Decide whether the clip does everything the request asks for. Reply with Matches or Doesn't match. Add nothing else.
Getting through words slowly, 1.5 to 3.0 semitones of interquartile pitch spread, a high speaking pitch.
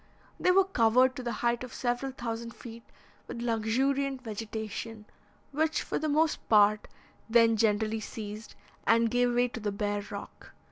Doesn't match